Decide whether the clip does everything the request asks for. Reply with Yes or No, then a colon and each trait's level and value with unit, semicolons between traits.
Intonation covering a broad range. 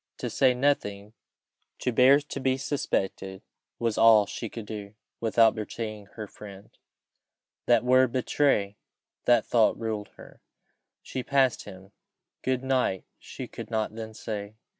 No: average, 3.6 semitones